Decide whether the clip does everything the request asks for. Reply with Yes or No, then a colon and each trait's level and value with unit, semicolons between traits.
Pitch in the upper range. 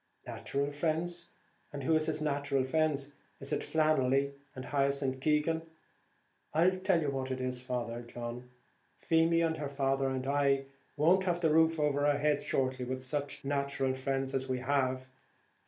No: medium, 140 Hz